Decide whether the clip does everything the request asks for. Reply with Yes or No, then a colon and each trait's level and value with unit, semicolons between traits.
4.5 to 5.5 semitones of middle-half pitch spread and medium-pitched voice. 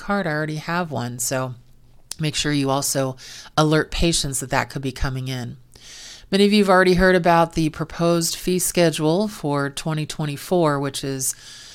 No: average, 4.1 semitones; medium, 150 Hz